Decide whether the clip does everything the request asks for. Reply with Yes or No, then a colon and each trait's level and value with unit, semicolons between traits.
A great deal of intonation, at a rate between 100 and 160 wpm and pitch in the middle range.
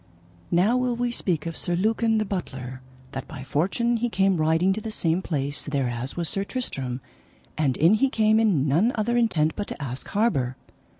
No: wide, 7.4 semitones; average, 190 wpm; medium, 180 Hz